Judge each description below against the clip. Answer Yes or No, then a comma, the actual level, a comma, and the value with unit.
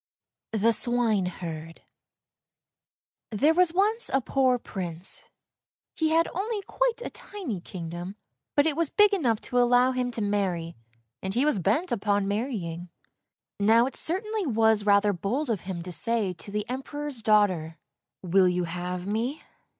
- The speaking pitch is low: No, high, 220 Hz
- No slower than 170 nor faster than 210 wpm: No, average, 150 wpm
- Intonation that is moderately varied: No, wide, 7.1 semitones